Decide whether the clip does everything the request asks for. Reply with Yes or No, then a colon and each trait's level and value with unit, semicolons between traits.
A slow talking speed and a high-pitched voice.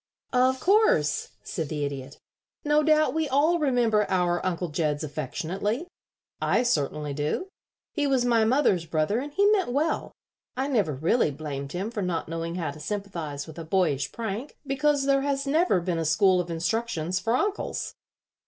No: average, 170 wpm; high, 195 Hz